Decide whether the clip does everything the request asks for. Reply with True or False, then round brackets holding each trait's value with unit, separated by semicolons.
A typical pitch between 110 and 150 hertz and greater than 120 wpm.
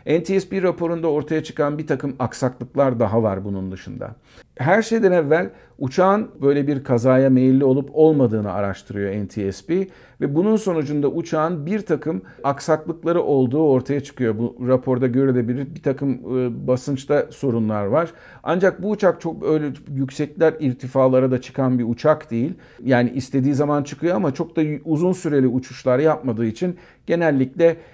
True (140 Hz; 140 wpm)